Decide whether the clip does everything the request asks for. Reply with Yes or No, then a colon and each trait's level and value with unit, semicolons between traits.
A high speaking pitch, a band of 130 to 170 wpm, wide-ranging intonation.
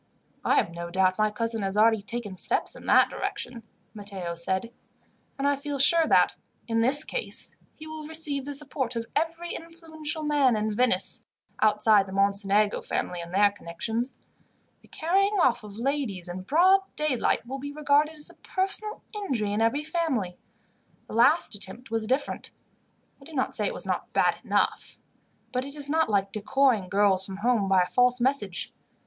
No: high, 240 Hz; average, 180 wpm; wide, 6.6 semitones